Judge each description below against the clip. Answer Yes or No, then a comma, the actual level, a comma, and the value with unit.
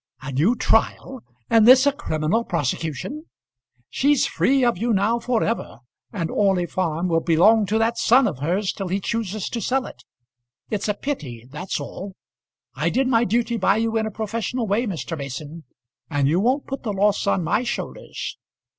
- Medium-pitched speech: No, high, 210 Hz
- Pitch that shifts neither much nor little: No, wide, 5.7 semitones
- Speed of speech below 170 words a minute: No, average, 180 wpm